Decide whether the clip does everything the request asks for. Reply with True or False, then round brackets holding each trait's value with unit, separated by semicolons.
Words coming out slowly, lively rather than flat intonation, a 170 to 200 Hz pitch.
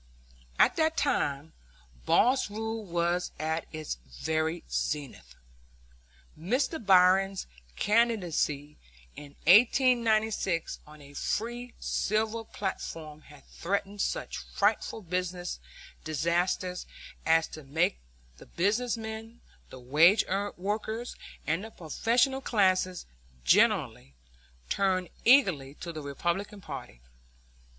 True (100 wpm; 5.8 semitones; 185 Hz)